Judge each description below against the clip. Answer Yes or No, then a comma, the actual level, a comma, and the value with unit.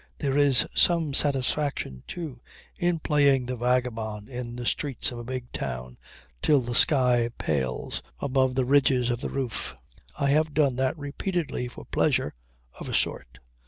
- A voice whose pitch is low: Yes, low, 130 Hz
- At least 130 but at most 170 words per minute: Yes, average, 160 wpm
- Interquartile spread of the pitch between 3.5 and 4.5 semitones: No, average, 3.0 semitones